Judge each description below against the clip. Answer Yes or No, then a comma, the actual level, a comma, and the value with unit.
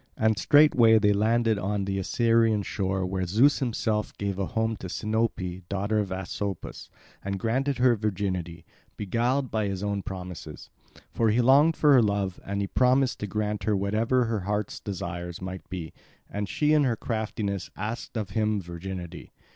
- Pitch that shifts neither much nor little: Yes, average, 3.1 semitones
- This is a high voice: No, low, 105 Hz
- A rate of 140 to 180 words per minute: Yes, average, 170 wpm